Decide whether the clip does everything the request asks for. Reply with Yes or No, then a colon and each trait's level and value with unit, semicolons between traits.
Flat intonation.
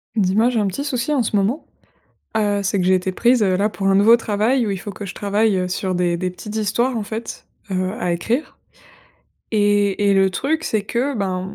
No: average, 3.2 semitones